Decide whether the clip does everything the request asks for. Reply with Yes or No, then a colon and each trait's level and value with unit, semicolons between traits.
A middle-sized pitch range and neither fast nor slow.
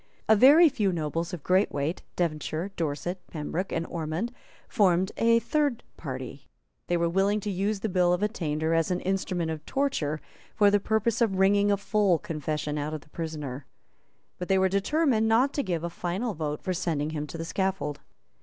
Yes: average, 4.5 semitones; average, 190 wpm